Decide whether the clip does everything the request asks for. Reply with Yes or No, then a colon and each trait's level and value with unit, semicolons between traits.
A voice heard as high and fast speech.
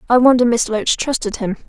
Yes: high, 235 Hz; fast, 215 wpm